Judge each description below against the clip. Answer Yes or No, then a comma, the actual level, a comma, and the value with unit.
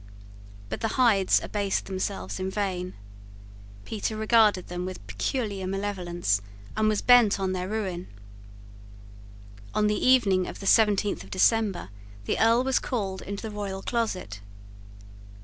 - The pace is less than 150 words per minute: Yes, slow, 135 wpm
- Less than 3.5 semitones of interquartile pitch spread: Yes, average, 2.7 semitones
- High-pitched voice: Yes, high, 200 Hz